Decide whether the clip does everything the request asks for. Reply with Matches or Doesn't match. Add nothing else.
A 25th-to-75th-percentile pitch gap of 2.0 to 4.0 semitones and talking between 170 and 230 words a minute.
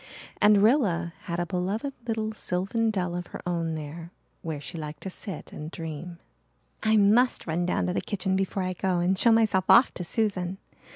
Matches